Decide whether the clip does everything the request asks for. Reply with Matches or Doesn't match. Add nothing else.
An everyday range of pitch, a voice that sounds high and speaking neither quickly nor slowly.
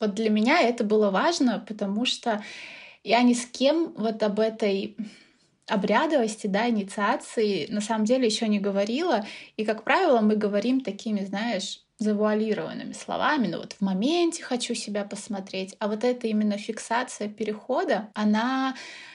Matches